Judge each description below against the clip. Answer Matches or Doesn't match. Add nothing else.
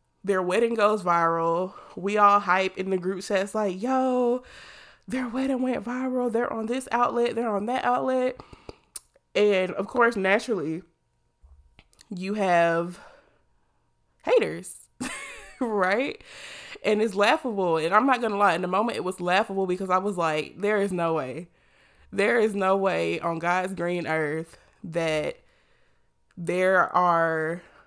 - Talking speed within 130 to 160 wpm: Matches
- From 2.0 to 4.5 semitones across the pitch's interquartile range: Doesn't match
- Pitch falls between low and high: Doesn't match